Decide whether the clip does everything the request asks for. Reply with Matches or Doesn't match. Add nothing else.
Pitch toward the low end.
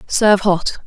Doesn't match